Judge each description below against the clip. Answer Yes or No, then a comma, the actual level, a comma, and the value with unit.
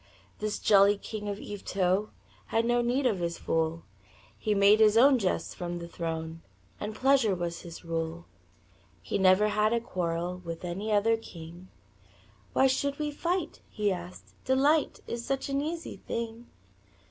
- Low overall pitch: No, high, 205 Hz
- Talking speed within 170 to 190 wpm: No, average, 160 wpm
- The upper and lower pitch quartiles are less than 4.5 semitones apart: No, wide, 5.4 semitones